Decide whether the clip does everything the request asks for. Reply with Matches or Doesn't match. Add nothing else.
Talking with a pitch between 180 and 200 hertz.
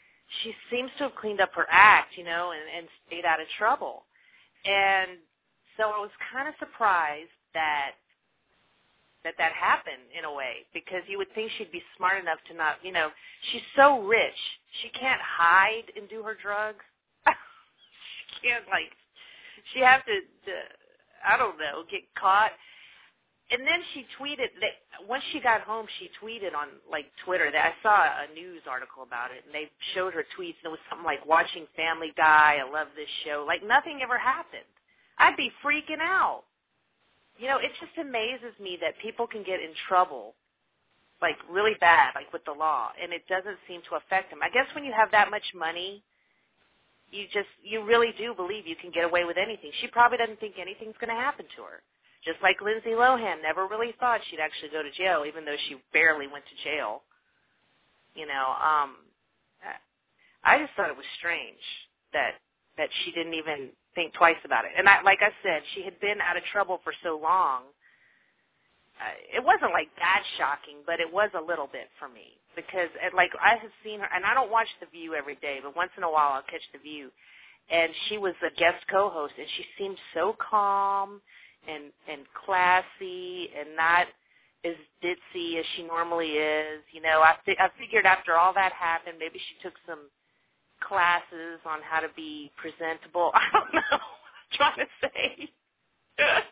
Matches